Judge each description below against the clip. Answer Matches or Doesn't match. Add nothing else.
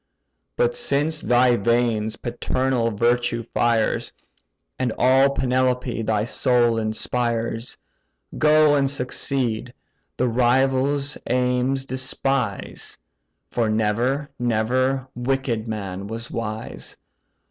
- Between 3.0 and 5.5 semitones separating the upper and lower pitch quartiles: Doesn't match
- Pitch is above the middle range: Doesn't match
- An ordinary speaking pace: Doesn't match